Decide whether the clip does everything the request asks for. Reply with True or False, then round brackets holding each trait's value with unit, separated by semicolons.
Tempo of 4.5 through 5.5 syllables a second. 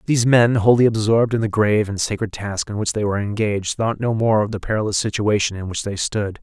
False (6.2 syllables/s)